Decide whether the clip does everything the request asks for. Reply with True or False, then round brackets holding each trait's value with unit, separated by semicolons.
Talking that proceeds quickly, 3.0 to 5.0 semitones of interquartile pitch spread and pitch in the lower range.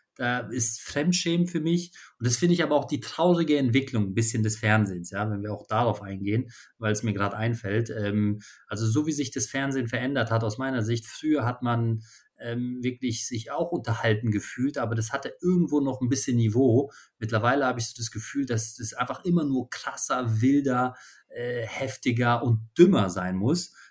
True (195 wpm; 3.6 semitones; 120 Hz)